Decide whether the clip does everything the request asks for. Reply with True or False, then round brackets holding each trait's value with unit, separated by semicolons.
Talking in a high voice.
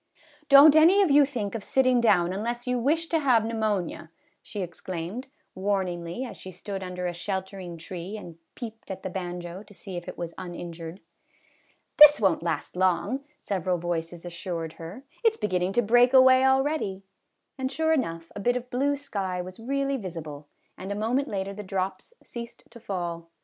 True (200 Hz)